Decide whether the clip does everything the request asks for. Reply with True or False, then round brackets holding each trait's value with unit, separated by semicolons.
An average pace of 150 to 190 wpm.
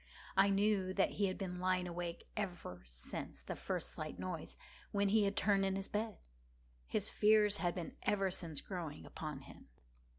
True (175 wpm)